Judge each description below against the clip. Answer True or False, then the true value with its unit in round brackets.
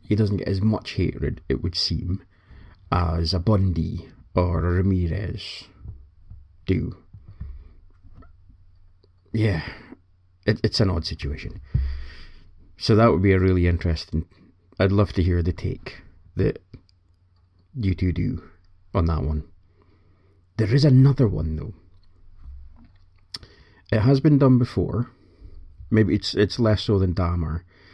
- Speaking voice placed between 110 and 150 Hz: False (90 Hz)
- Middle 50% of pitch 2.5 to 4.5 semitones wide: True (2.8 semitones)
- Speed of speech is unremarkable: False (125 wpm)